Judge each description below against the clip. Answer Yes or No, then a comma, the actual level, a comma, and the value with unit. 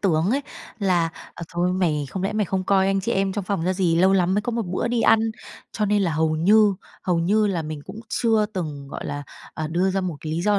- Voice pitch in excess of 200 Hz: No, high, 190 Hz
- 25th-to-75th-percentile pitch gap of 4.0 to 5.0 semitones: No, average, 3.5 semitones